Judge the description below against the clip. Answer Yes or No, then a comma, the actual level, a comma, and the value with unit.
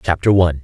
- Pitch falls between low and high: No, very low, 85 Hz